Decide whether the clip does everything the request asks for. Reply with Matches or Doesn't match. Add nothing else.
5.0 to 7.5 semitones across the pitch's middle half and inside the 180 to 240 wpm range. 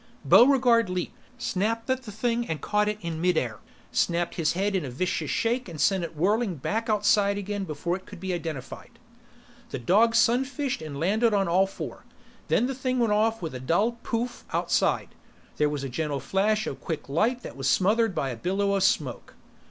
Matches